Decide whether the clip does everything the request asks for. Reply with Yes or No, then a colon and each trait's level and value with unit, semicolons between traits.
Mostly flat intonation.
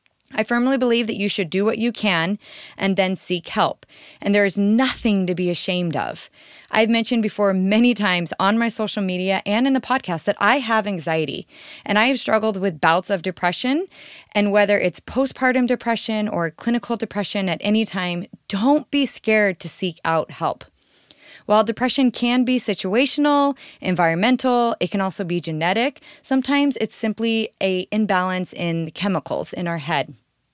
No: average, 4.8 semitones